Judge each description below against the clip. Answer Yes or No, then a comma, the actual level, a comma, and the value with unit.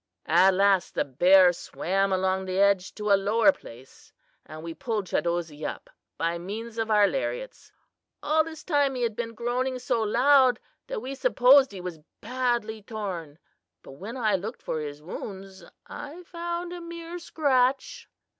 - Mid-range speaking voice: No, high, 220 Hz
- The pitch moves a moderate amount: No, wide, 6.1 semitones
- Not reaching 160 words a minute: No, average, 165 wpm